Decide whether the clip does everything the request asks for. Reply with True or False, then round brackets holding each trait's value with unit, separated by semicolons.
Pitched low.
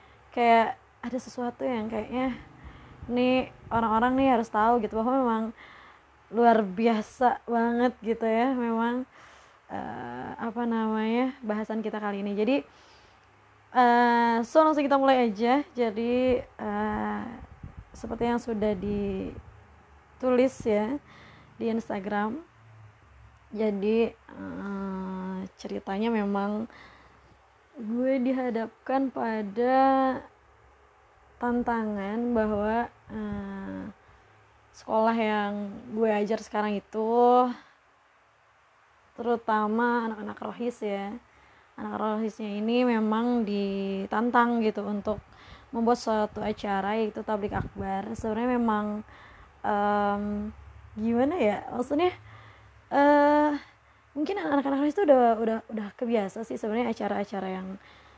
False (225 Hz)